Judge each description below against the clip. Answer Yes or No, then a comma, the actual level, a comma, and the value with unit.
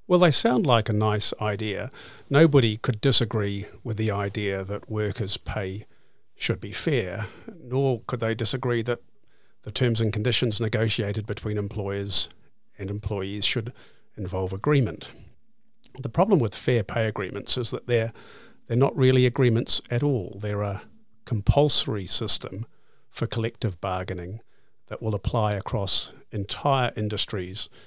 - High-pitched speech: No, low, 110 Hz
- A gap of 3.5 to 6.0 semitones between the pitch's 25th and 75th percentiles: No, average, 3.1 semitones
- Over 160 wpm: No, average, 140 wpm